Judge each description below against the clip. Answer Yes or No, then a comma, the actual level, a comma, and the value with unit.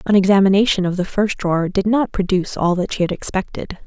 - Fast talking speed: Yes, fast, 220 wpm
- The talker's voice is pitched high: Yes, high, 195 Hz